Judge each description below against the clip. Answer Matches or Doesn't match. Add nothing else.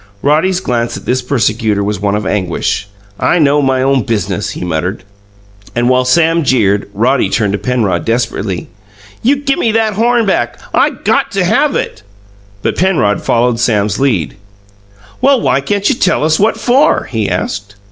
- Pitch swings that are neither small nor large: Doesn't match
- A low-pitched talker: Matches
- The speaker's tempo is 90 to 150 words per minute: Doesn't match